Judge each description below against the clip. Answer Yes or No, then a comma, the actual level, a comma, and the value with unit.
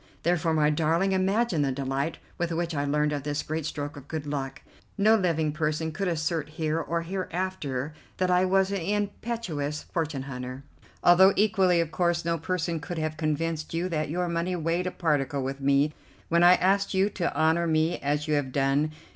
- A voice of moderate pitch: Yes, medium, 160 Hz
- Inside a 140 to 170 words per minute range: No, average, 190 wpm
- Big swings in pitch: No, average, 3.3 semitones